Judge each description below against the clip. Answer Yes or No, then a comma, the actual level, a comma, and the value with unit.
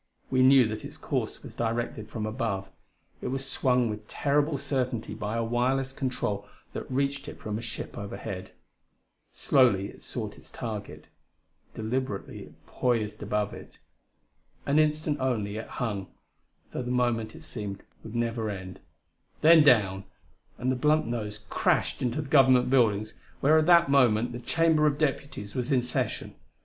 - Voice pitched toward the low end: Yes, low, 120 Hz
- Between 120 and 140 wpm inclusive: No, average, 160 wpm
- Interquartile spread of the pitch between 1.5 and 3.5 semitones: No, average, 4.0 semitones